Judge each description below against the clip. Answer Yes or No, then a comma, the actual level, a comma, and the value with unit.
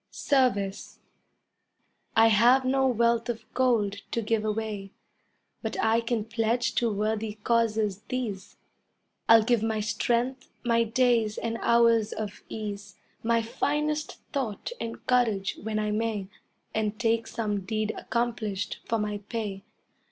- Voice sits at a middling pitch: No, high, 225 Hz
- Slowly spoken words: Yes, slow, 130 wpm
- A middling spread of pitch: No, narrow, 1.9 semitones